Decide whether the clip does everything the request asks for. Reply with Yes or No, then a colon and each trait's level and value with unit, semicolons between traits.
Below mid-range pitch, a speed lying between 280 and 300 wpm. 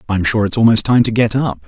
Yes: low, 110 Hz; fast, 285 wpm